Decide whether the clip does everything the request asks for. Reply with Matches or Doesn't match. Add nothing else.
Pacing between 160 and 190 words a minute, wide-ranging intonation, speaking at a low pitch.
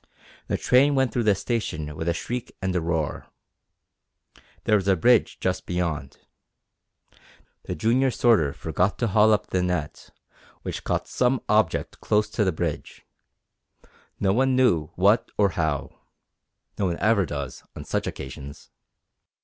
Doesn't match